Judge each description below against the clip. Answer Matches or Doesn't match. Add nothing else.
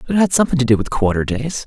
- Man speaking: Matches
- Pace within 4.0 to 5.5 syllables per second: Doesn't match